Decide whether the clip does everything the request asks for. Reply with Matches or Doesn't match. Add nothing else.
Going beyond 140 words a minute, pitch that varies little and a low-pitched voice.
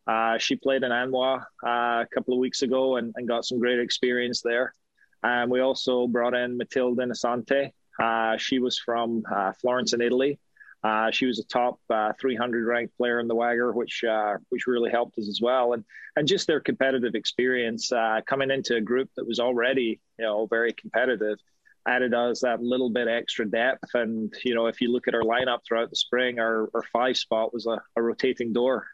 Matches